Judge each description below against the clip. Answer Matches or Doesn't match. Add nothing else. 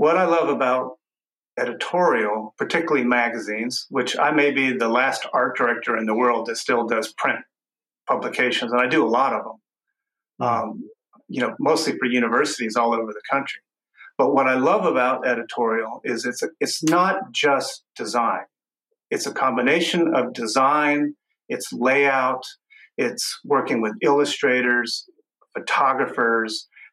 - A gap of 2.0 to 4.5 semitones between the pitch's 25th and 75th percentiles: Matches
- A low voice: Matches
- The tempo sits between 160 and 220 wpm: Doesn't match